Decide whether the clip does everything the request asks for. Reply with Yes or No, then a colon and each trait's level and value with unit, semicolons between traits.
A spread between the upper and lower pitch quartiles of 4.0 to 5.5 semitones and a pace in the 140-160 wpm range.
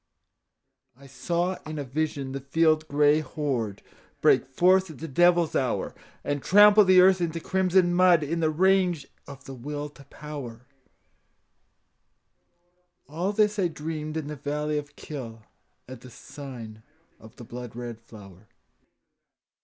Yes: average, 4.7 semitones; average, 145 wpm